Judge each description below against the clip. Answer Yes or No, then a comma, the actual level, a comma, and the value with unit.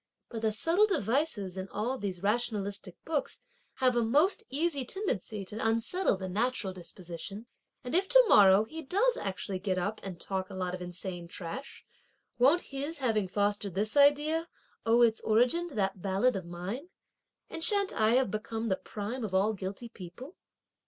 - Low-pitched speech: No, high, 220 Hz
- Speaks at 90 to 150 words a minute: No, average, 170 wpm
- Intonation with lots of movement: Yes, wide, 6.2 semitones